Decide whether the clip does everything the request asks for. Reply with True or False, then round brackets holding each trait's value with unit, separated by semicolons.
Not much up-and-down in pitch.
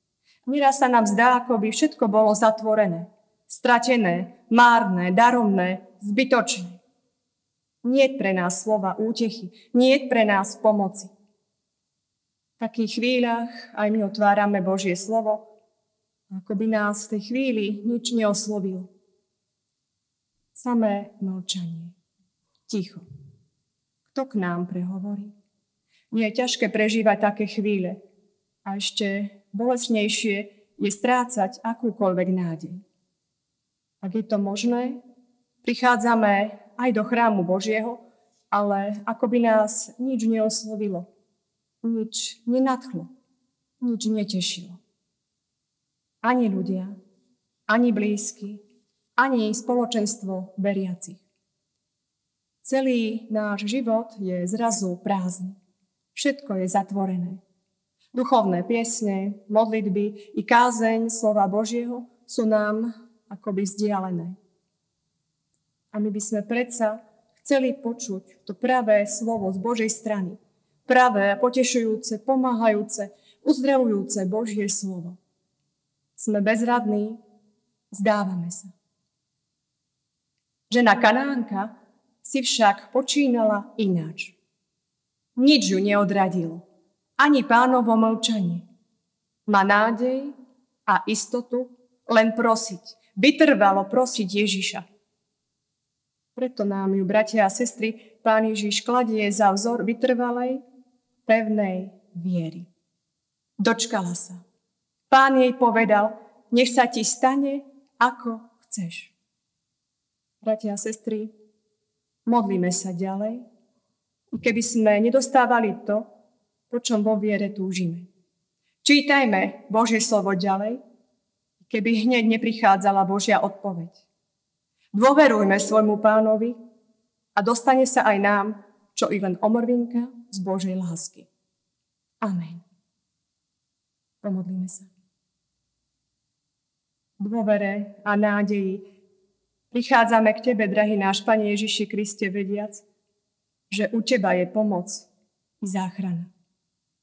False (3.2 semitones)